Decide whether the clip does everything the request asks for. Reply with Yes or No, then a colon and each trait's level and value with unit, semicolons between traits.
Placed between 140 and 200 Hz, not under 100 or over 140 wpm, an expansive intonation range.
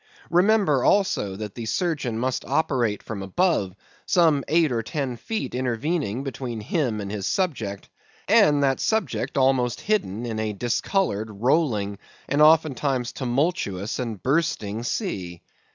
No: low, 130 Hz; slow, 135 wpm; wide, 6.4 semitones